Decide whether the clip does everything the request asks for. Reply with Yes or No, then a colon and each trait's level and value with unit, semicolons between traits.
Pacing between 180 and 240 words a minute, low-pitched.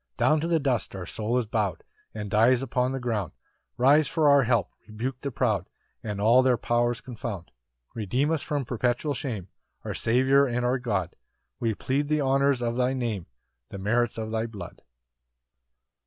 Yes: average, 185 wpm; low, 120 Hz